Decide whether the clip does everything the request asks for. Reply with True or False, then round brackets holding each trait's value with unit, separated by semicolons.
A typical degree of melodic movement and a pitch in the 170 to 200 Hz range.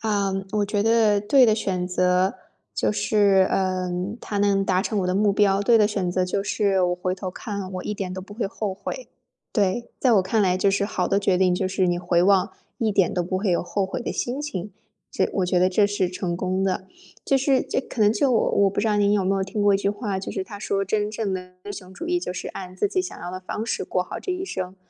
False (2.1 semitones; 195 Hz)